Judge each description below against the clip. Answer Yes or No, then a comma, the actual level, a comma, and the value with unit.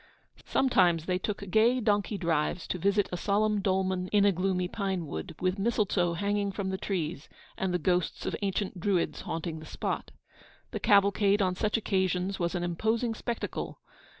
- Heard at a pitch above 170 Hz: Yes, high, 190 Hz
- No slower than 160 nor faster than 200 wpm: Yes, average, 170 wpm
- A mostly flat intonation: Yes, narrow, 2.3 semitones